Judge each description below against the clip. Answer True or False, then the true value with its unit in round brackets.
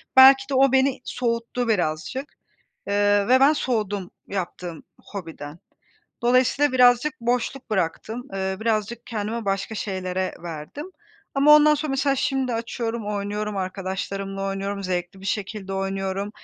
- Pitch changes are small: False (4.8 semitones)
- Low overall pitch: False (210 Hz)